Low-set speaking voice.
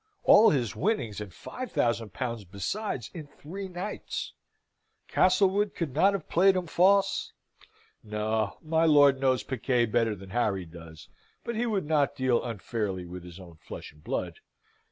Yes: low, 130 Hz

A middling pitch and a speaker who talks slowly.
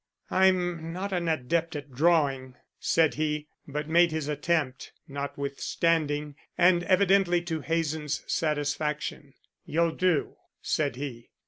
Yes: medium, 155 Hz; slow, 115 wpm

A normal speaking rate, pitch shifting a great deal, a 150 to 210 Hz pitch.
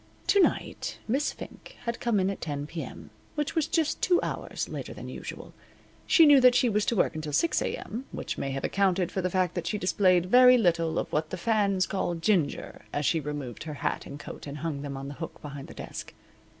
No: fast, 225 wpm; wide, 7.4 semitones; medium, 185 Hz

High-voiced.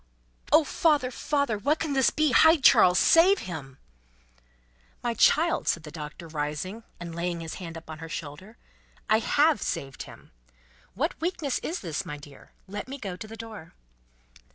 Yes: high, 205 Hz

